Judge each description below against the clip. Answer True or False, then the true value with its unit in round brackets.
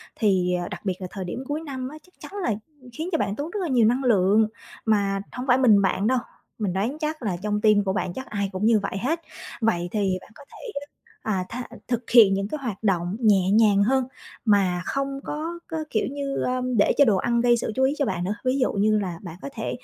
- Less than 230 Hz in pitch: True (220 Hz)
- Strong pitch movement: False (5.0 semitones)